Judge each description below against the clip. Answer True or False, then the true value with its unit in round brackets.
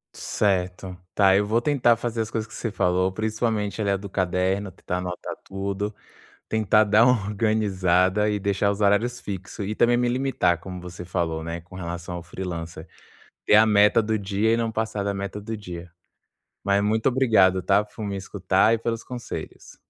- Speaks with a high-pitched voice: False (100 Hz)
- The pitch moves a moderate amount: True (3.0 semitones)